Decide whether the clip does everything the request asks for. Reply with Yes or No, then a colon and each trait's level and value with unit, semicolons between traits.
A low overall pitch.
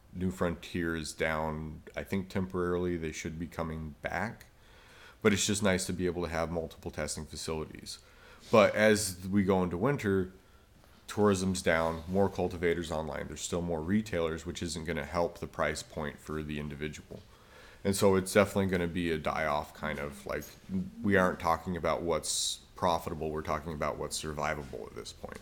Yes: very low, 85 Hz